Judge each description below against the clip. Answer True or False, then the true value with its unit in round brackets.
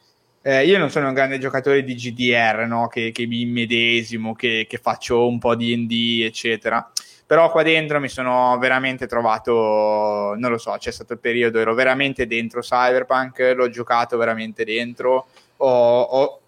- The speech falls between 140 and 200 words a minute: True (170 wpm)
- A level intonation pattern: True (1.9 semitones)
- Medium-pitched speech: False (120 Hz)